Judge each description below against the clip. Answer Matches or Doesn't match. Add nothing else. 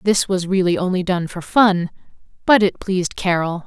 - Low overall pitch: Doesn't match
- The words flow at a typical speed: Matches